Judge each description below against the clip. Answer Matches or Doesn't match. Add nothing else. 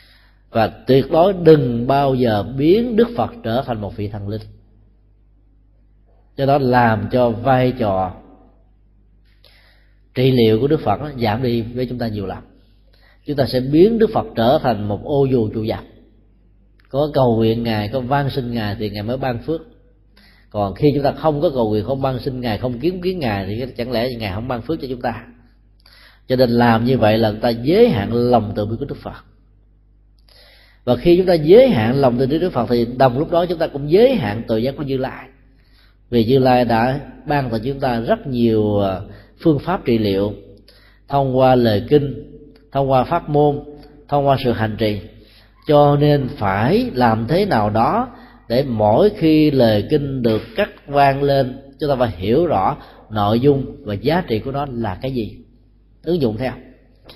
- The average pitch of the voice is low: Matches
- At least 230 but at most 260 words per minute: Doesn't match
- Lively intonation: Doesn't match